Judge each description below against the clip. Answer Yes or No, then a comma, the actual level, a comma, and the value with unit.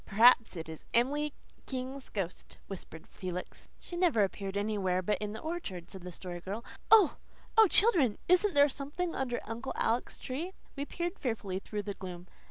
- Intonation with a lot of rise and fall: Yes, wide, 7.3 semitones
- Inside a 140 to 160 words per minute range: No, average, 175 wpm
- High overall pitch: Yes, high, 230 Hz